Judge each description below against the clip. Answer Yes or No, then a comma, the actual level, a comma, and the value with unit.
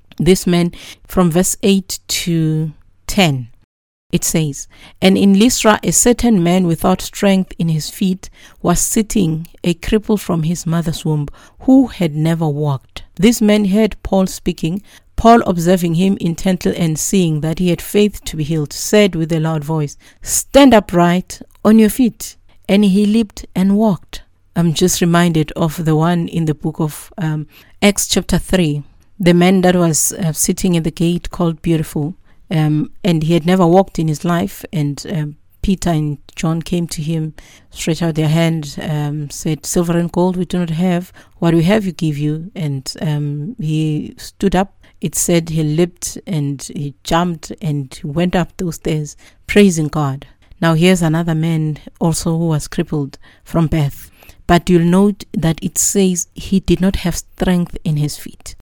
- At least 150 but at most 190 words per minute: Yes, average, 175 wpm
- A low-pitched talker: No, medium, 170 Hz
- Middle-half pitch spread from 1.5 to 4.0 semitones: Yes, average, 3.3 semitones